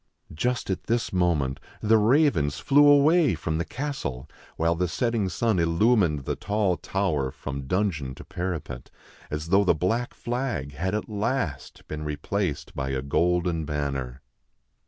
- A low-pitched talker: Yes, very low, 90 Hz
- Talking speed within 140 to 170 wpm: Yes, average, 150 wpm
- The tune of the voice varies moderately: No, wide, 7.0 semitones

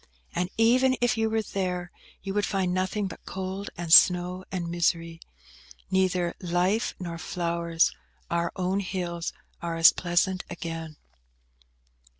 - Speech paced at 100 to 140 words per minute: Yes, slow, 135 wpm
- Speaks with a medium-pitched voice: Yes, medium, 180 Hz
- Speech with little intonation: Yes, narrow, 2.0 semitones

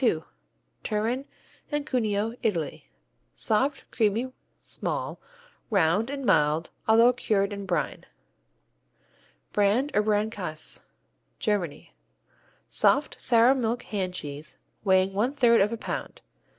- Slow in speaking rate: Yes, slow, 110 wpm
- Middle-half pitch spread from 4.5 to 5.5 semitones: No, average, 4.0 semitones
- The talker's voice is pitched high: Yes, high, 210 Hz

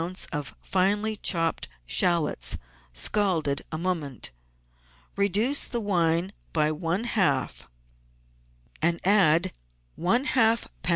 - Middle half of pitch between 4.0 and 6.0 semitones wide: Yes, average, 4.6 semitones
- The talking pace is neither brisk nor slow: No, slow, 100 wpm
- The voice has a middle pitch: Yes, medium, 180 Hz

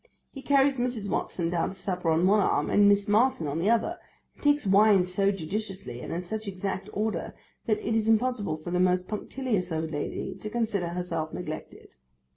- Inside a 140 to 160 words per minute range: No, average, 195 wpm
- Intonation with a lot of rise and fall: No, average, 3.7 semitones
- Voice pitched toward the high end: Yes, high, 200 Hz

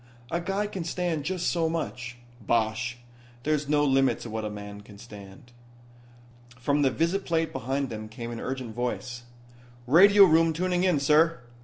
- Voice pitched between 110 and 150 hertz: Yes, medium, 140 Hz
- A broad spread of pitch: Yes, wide, 5.8 semitones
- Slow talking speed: No, average, 160 wpm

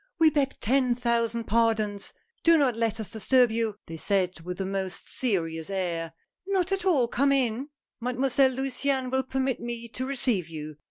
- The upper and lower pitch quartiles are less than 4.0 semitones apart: No, average, 5.0 semitones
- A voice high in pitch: Yes, high, 235 Hz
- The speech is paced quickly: No, average, 170 wpm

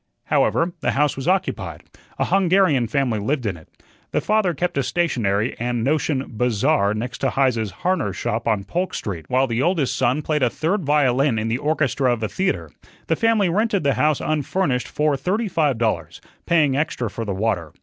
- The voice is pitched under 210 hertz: Yes, low, 135 Hz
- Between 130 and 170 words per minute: No, average, 190 wpm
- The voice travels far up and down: Yes, wide, 6.2 semitones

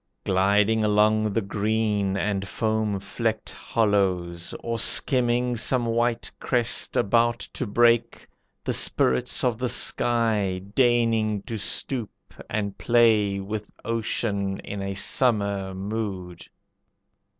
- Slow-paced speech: Yes, slow, 110 wpm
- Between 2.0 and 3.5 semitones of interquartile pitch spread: Yes, average, 2.8 semitones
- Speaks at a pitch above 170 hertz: No, low, 110 Hz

